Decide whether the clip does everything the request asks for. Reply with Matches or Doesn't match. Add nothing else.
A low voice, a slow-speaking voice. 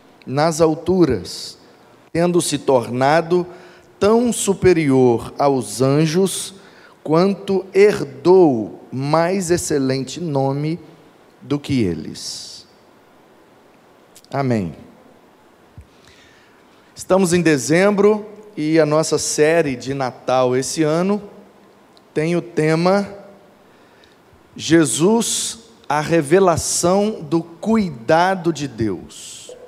Doesn't match